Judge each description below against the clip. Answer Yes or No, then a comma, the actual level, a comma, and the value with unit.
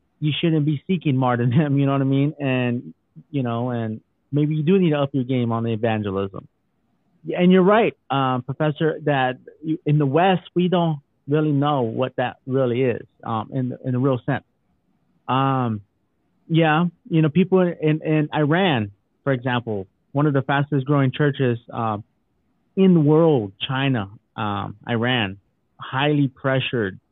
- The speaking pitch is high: No, low, 135 Hz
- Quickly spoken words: No, average, 165 wpm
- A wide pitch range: No, average, 4.1 semitones